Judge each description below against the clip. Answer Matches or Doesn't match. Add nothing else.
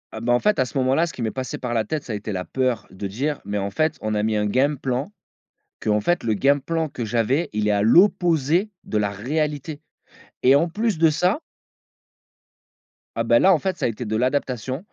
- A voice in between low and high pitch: Doesn't match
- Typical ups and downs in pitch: Doesn't match